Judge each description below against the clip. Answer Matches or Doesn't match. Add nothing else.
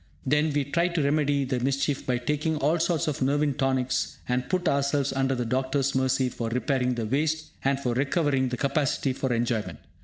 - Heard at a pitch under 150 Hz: Matches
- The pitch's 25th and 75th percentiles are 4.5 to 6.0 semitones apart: Doesn't match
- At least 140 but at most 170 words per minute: Doesn't match